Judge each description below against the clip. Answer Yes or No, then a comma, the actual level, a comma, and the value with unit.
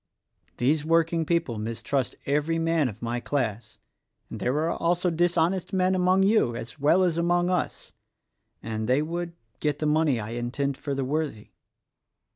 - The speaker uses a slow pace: No, average, 160 wpm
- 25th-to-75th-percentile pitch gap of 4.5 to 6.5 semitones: Yes, wide, 5.5 semitones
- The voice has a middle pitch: Yes, medium, 155 Hz